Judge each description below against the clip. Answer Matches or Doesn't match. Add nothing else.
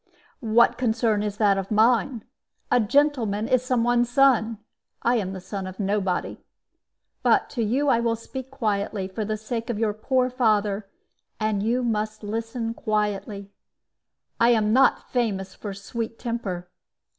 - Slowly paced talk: Doesn't match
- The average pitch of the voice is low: Doesn't match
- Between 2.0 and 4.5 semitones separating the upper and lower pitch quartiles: Matches